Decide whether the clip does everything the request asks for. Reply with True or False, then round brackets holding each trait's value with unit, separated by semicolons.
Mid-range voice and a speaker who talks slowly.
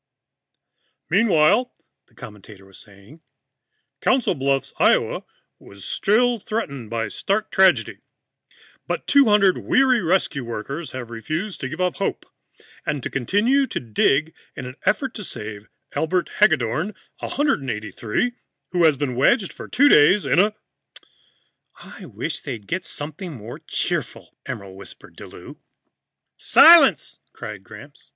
True (155 Hz; 130 wpm)